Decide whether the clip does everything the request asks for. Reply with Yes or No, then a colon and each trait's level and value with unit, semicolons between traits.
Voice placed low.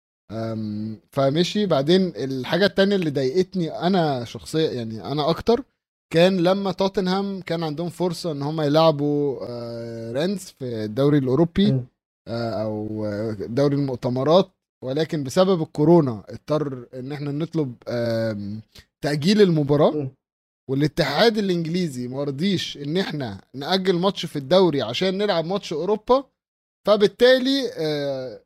No: medium, 150 Hz